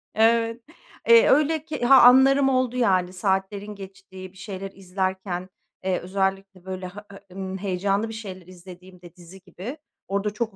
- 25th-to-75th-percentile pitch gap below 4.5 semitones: Yes, average, 3.4 semitones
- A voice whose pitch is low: No, high, 195 Hz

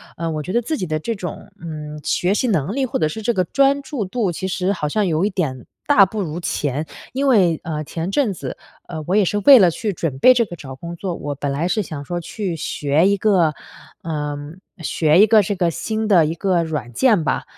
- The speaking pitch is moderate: Yes, medium, 175 Hz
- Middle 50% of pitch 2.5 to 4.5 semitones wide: No, average, 5.2 semitones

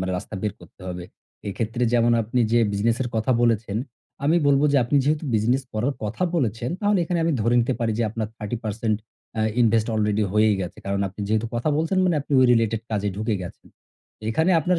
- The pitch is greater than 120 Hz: No, low, 115 Hz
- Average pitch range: Yes, average, 3.7 semitones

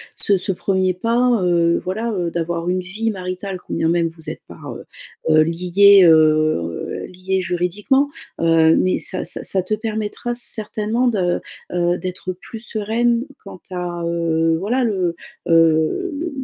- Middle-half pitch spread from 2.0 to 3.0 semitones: No, average, 4.1 semitones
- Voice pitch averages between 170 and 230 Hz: Yes, medium, 185 Hz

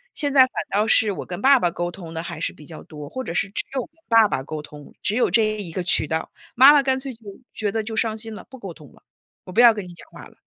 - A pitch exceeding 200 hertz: Yes, high, 210 Hz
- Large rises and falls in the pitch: Yes, wide, 5.7 semitones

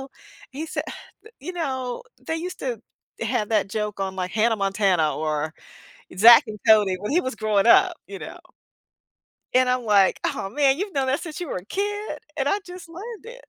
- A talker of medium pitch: No, very high, 250 Hz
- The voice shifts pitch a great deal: Yes, wide, 8.8 semitones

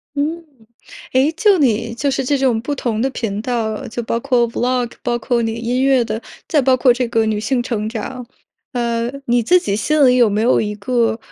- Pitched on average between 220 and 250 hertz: Yes, high, 240 Hz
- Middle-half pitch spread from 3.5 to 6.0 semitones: No, narrow, 2.6 semitones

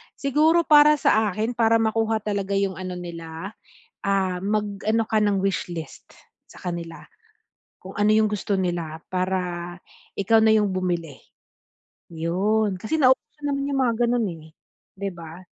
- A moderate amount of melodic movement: Yes, average, 3.9 semitones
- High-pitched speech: Yes, high, 200 Hz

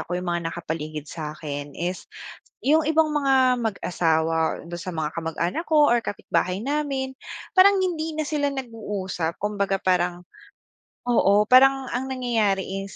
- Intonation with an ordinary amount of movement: No, wide, 7.8 semitones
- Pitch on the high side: Yes, high, 200 Hz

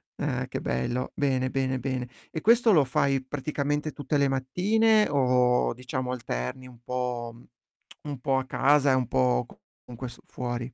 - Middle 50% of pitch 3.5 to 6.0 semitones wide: No, narrow, 2.5 semitones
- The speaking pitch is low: Yes, low, 130 Hz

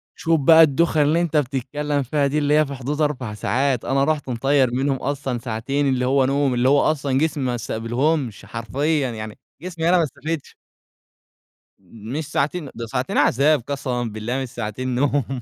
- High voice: No, low, 135 Hz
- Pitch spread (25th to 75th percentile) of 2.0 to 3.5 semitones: Yes, average, 3.1 semitones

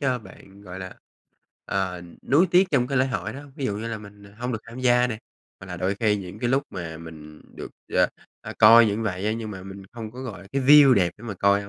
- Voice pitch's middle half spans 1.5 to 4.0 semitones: No, average, 4.5 semitones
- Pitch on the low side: Yes, low, 105 Hz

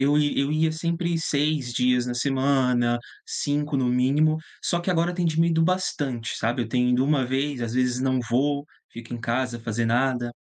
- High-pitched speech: No, low, 135 Hz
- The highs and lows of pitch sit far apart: No, average, 3.8 semitones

